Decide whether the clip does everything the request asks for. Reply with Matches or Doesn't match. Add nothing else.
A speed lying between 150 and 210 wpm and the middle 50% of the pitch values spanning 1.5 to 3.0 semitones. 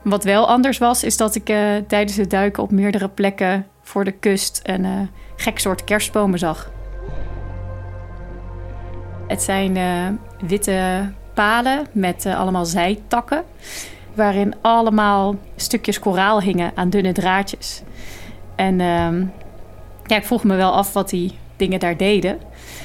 Doesn't match